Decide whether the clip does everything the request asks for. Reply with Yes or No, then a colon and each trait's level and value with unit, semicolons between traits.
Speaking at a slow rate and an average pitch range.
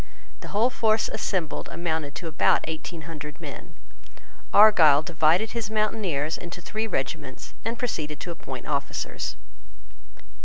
No: slow, 125 wpm; wide, 5.9 semitones